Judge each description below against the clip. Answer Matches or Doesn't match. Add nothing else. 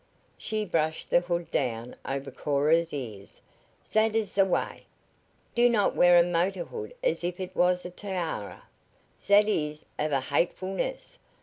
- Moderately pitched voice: Matches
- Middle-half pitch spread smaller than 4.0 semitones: Doesn't match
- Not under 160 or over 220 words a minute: Doesn't match